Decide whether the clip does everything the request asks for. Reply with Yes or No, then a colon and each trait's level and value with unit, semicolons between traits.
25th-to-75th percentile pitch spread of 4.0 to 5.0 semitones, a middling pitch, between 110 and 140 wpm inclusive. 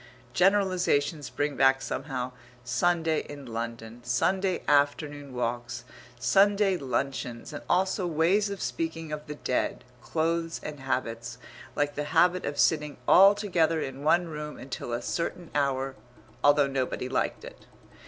Yes: average, 4.4 semitones; medium, 145 Hz; slow, 135 wpm